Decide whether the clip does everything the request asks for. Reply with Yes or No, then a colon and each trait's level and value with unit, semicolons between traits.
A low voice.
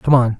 Yes: low, 125 Hz